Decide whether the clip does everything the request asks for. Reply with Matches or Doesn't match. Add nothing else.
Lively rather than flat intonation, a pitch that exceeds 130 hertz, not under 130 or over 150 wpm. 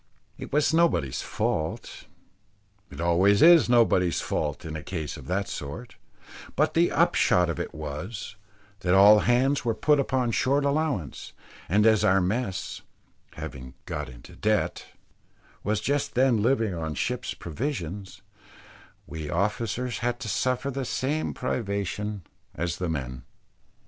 Doesn't match